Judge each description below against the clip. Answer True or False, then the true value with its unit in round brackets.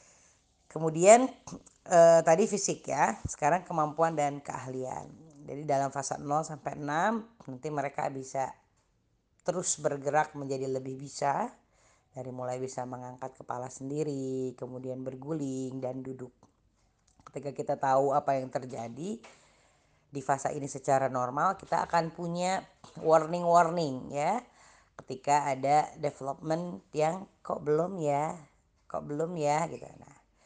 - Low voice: False (145 Hz)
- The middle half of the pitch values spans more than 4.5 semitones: False (3.6 semitones)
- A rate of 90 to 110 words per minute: False (120 wpm)